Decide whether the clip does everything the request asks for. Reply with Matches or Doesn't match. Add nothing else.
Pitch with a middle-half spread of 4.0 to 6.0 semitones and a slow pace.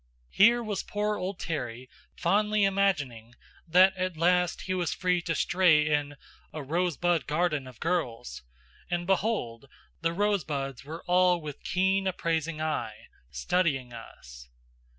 Matches